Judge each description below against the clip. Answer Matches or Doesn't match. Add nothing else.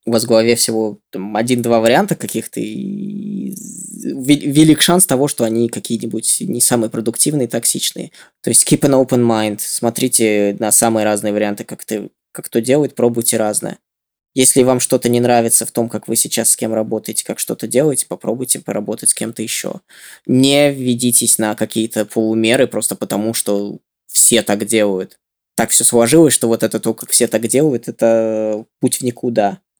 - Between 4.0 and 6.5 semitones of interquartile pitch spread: Doesn't match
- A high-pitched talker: Doesn't match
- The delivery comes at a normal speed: Doesn't match